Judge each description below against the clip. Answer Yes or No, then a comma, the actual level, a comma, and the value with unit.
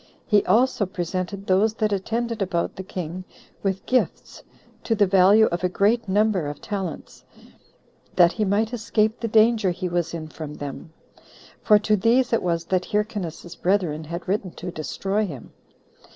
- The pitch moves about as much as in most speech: Yes, average, 3.6 semitones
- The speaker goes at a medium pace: Yes, average, 165 wpm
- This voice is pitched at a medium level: No, high, 195 Hz